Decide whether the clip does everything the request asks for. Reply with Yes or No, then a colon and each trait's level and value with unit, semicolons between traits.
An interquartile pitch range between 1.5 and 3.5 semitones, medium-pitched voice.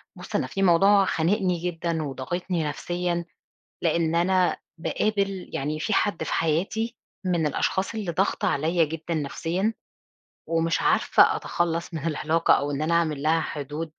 Yes: narrow, 2.6 semitones; medium, 170 Hz